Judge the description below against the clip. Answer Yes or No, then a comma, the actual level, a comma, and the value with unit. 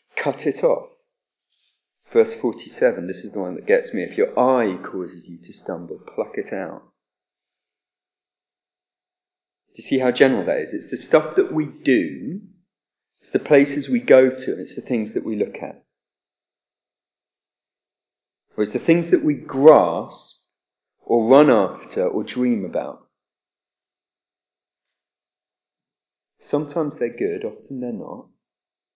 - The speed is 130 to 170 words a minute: Yes, average, 140 wpm